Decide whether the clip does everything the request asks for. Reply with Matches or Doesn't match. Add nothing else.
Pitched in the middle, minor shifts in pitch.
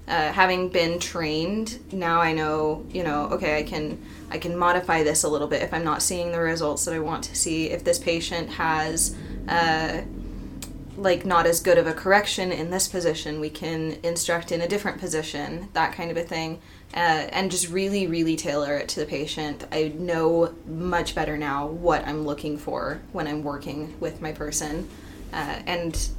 Matches